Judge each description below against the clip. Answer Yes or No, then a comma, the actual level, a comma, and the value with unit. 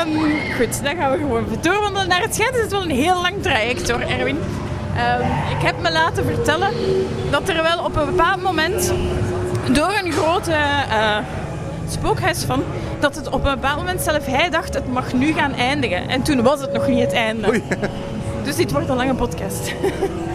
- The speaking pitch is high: Yes, very high, 300 Hz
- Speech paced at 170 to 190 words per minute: No, fast, 200 wpm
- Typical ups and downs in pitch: No, wide, 9.0 semitones